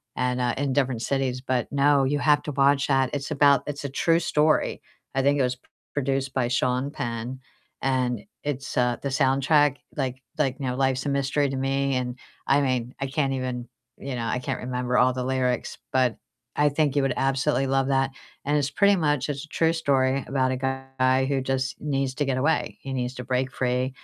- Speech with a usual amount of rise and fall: No, narrow, 1.7 semitones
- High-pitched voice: No, low, 135 Hz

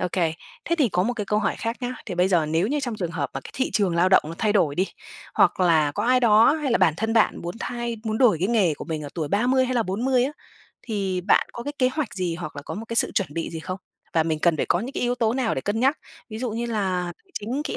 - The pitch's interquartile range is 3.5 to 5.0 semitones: No, wide, 5.6 semitones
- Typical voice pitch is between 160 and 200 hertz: No, high, 210 Hz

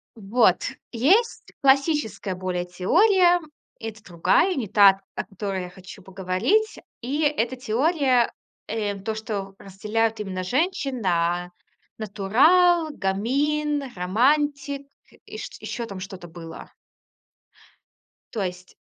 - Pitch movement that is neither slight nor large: No, wide, 6.9 semitones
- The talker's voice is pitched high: Yes, high, 220 Hz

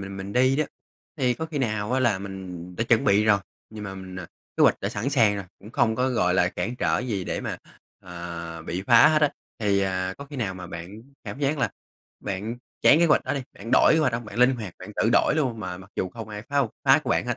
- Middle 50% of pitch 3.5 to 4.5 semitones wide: No, average, 5.0 semitones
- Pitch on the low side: Yes, low, 105 Hz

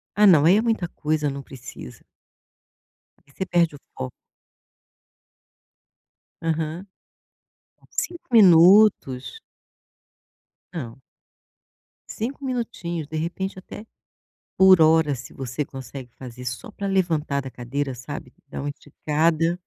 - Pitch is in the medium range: Yes, medium, 160 Hz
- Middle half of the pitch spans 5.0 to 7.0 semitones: Yes, wide, 5.5 semitones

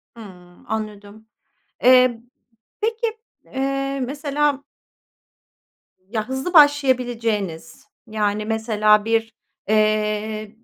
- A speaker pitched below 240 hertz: Yes, high, 225 Hz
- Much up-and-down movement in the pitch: No, average, 4.3 semitones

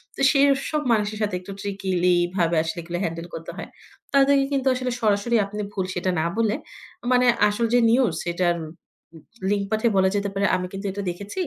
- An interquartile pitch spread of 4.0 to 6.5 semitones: Yes, average, 4.4 semitones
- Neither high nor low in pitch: No, high, 200 Hz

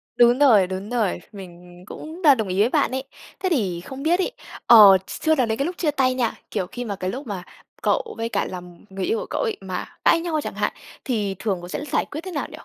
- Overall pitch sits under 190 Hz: No, high, 235 Hz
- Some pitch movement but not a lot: No, wide, 8.0 semitones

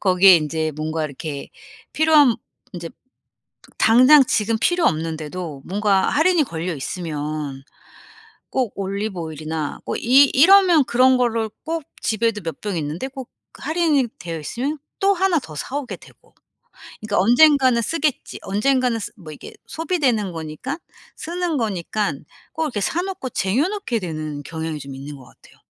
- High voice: Yes, high, 215 Hz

